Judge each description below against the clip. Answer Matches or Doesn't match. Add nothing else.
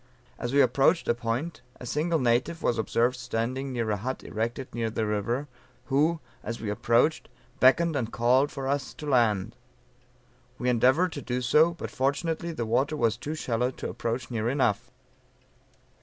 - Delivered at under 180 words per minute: Matches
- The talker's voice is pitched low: Matches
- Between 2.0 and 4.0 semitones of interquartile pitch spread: Matches